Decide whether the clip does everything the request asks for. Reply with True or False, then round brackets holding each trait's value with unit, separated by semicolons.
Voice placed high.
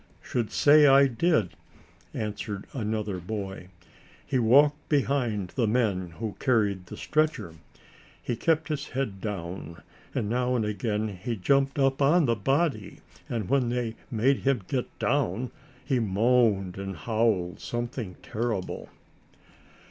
False (115 Hz)